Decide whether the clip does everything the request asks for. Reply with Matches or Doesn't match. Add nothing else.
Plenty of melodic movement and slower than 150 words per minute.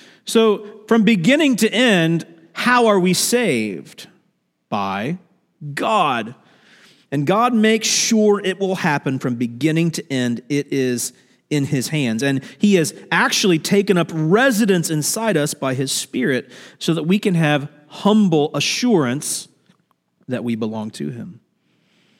Matches